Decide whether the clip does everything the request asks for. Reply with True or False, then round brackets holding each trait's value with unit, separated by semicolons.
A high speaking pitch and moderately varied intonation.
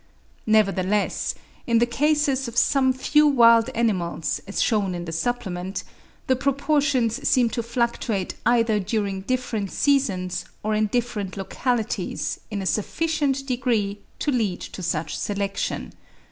True (230 Hz; 4.5 semitones)